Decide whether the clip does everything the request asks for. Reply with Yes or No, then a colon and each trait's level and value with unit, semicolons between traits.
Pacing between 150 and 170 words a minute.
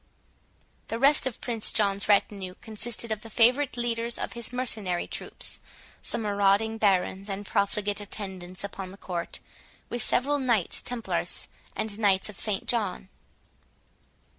No: average, 140 wpm